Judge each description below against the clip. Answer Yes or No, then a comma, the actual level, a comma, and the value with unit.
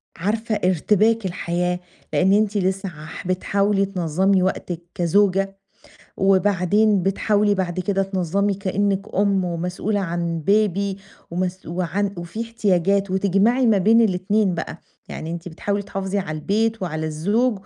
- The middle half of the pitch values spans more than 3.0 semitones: No, narrow, 2.4 semitones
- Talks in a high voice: Yes, high, 195 Hz